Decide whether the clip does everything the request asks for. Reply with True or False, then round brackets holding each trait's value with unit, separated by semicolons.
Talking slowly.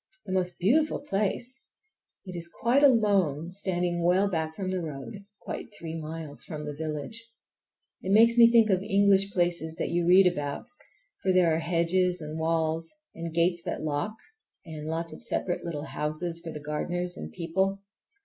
False (170 wpm)